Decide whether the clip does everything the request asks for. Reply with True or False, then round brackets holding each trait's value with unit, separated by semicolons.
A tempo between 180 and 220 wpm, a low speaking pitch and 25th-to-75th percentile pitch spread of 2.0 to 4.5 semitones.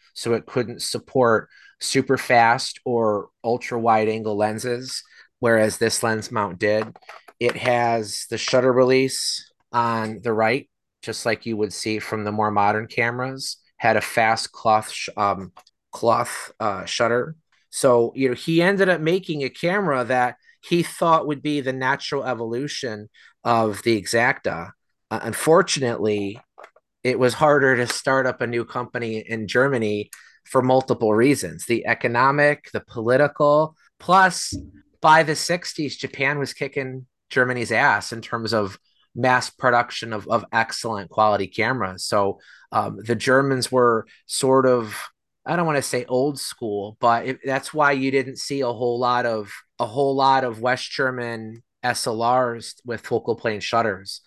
False (155 wpm; 125 Hz; 3.4 semitones)